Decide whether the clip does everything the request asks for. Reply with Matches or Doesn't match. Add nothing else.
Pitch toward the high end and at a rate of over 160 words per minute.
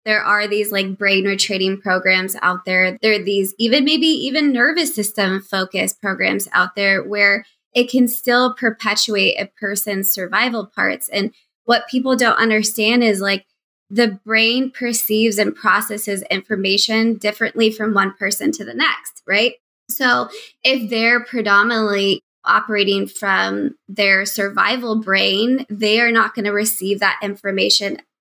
Doesn't match